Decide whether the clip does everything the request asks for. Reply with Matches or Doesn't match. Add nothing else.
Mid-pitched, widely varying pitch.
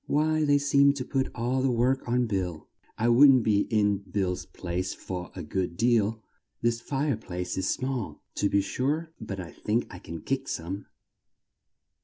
Doesn't match